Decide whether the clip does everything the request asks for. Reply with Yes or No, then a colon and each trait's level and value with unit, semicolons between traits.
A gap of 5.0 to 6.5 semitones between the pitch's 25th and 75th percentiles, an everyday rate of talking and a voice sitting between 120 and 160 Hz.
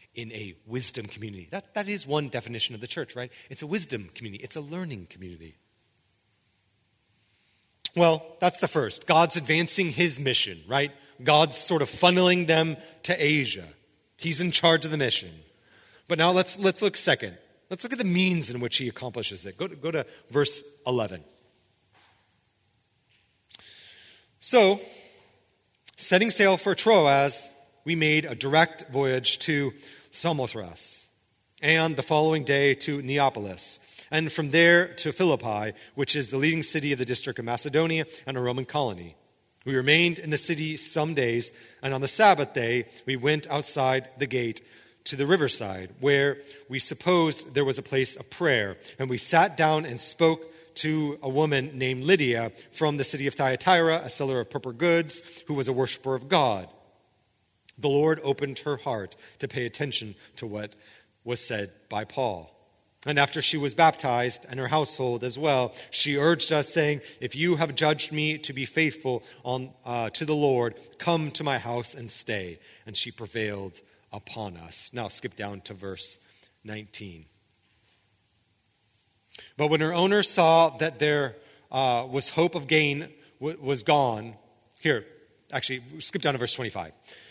Yes: average, 5.3 semitones; average, 170 wpm; low, 135 Hz